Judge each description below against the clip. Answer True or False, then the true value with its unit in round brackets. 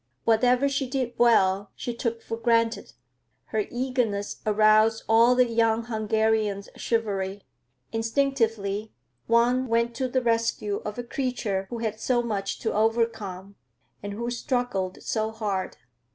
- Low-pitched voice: False (225 Hz)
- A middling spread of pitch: False (2.3 semitones)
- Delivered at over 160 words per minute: False (135 wpm)